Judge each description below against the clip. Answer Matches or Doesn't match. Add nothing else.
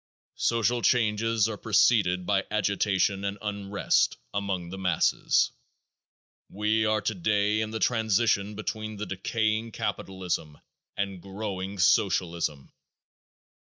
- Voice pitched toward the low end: Matches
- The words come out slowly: Matches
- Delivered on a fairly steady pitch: Matches